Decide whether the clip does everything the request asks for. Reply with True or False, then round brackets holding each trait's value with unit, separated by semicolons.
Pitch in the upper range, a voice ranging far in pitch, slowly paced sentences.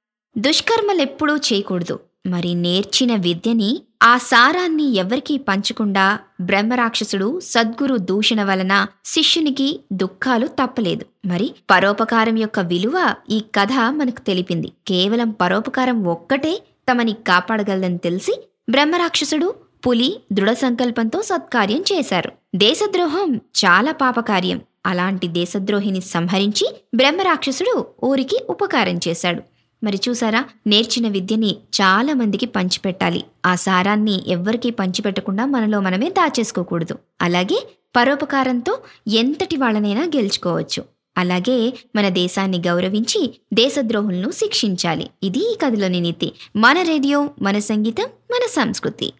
False (225 Hz; 5.9 semitones; 100 wpm)